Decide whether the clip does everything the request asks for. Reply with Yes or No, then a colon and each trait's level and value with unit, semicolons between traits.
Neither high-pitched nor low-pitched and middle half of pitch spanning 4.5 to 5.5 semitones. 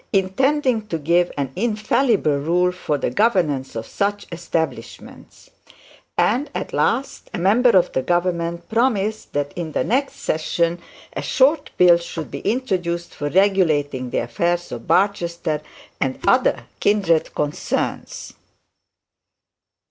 Yes: medium, 175 Hz; average, 5.0 semitones